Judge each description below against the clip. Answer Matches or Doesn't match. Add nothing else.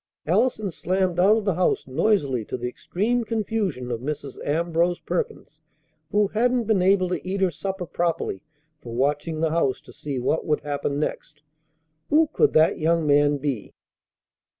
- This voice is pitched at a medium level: Matches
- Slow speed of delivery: Doesn't match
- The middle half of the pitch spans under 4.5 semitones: Doesn't match